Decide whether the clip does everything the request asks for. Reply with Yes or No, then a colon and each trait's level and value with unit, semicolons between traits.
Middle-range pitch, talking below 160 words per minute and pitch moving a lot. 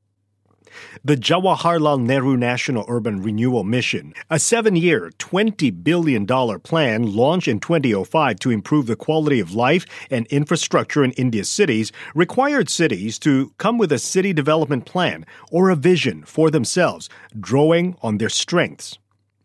Yes: medium, 145 Hz; average, 140 wpm; wide, 6.7 semitones